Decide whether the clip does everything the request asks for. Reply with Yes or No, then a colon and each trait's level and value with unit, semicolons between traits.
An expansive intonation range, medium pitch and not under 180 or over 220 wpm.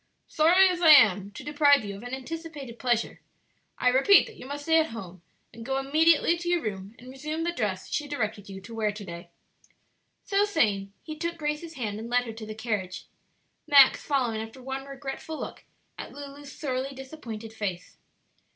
No: wide, 5.8 semitones; very high, 265 Hz; average, 190 wpm